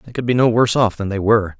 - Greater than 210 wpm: Yes, fast, 340 wpm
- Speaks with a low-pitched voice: Yes, low, 110 Hz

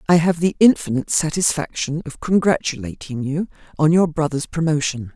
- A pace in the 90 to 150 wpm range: Yes, average, 140 wpm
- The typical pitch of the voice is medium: Yes, medium, 155 Hz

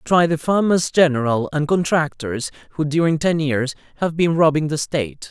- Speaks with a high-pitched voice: No, medium, 155 Hz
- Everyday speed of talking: Yes, average, 170 wpm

